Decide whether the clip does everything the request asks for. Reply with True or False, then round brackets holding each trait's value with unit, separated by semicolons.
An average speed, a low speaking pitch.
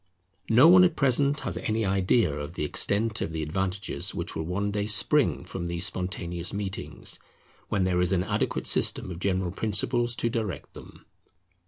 True (175 wpm; 95 Hz)